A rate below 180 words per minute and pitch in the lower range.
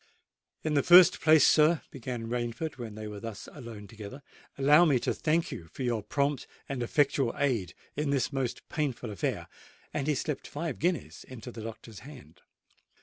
Yes: average, 170 wpm; low, 130 Hz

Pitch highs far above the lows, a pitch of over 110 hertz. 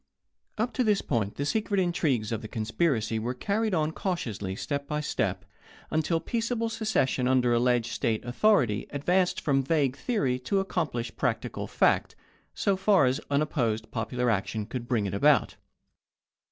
Yes: wide, 7.6 semitones; low, 135 Hz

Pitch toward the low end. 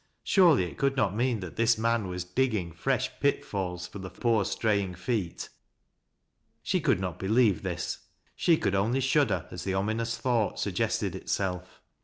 Yes: low, 105 Hz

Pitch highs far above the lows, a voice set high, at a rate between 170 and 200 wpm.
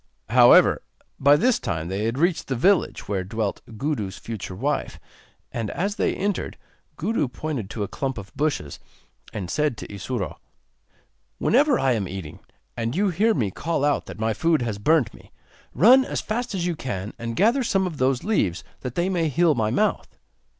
No: wide, 8.5 semitones; low, 135 Hz; average, 185 wpm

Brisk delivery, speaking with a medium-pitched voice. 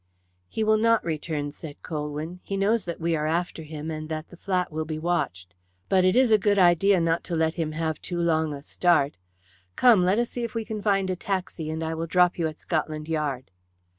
Yes: fast, 225 wpm; medium, 165 Hz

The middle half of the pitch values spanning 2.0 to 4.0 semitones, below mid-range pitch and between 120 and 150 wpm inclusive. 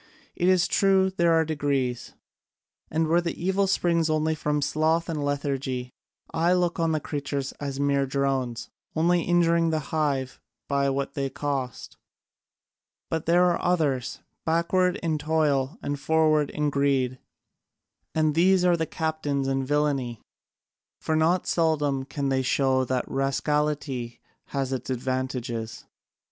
No: average, 3.3 semitones; medium, 150 Hz; average, 140 wpm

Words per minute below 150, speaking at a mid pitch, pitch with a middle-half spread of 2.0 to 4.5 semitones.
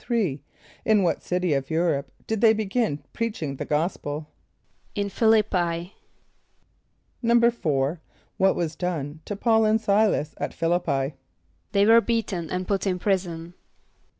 No: average, 140 wpm; medium, 180 Hz; average, 5.1 semitones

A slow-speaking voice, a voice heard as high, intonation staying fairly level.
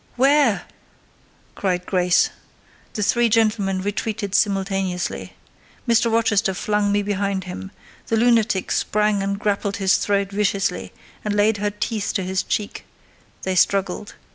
Yes: slow, 130 wpm; high, 205 Hz; narrow, 1.7 semitones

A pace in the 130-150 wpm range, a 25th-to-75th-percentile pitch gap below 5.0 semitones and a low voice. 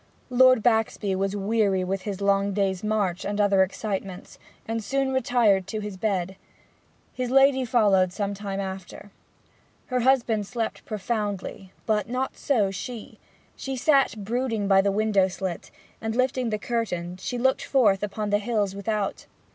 No: average, 145 wpm; average, 3.4 semitones; high, 210 Hz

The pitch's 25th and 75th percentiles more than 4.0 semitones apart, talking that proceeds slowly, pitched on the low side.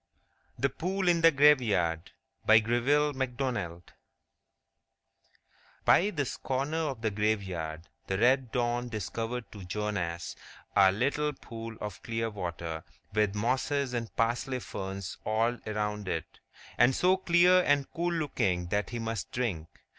Yes: average, 5.3 semitones; slow, 130 wpm; low, 115 Hz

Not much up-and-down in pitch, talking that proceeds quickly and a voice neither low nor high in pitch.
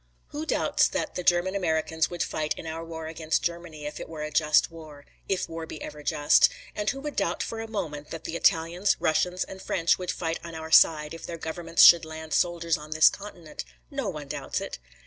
Yes: narrow, 2.0 semitones; fast, 220 wpm; medium, 165 Hz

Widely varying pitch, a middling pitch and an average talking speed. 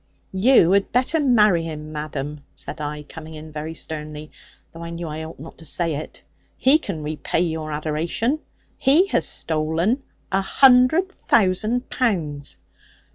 Yes: wide, 6.7 semitones; medium, 165 Hz; average, 150 wpm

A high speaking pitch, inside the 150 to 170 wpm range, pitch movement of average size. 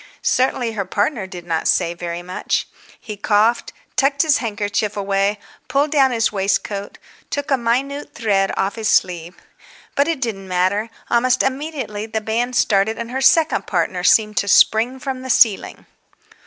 Yes: high, 220 Hz; average, 160 wpm; average, 4.7 semitones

